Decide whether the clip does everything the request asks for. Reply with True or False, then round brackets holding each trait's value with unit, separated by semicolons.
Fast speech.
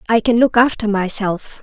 False (185 wpm)